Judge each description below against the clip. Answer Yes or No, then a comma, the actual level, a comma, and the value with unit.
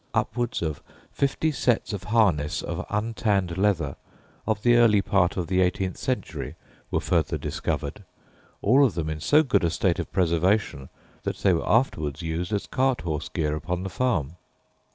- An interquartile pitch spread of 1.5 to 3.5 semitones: No, average, 5.2 semitones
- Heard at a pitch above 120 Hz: No, very low, 95 Hz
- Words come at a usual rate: Yes, average, 170 wpm